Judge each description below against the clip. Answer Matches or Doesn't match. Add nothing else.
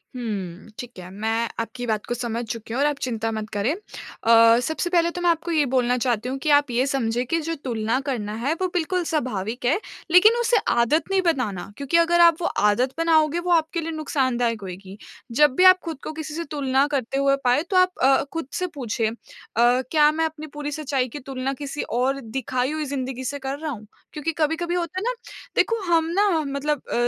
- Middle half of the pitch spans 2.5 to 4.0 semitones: Doesn't match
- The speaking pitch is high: Matches